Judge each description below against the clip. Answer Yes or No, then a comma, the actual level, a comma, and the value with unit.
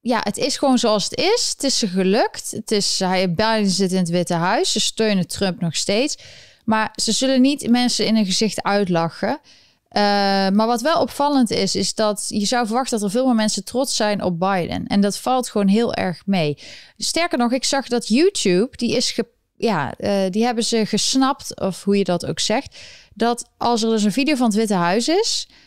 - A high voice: Yes, high, 220 Hz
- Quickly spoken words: Yes, fast, 215 wpm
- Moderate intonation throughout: Yes, average, 3.7 semitones